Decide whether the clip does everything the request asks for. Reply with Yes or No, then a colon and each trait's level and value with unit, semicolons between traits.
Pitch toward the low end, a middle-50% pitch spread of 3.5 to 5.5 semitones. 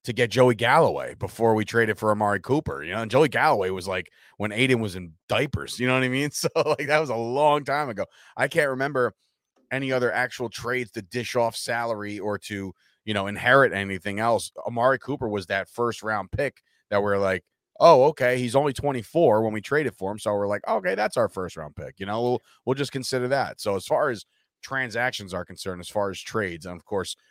Yes: low, 115 Hz; average, 4.0 semitones